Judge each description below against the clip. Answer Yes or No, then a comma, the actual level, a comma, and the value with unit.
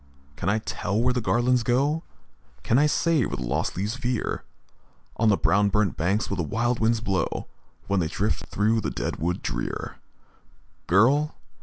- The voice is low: Yes, low, 110 Hz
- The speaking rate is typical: Yes, average, 175 wpm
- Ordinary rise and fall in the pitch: Yes, average, 4.3 semitones